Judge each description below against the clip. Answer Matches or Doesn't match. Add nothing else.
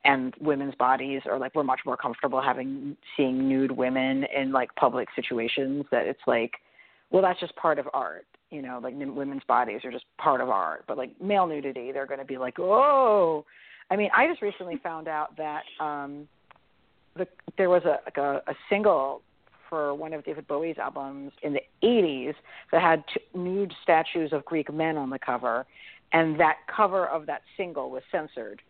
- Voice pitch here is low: Doesn't match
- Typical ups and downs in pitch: Matches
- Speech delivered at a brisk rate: Doesn't match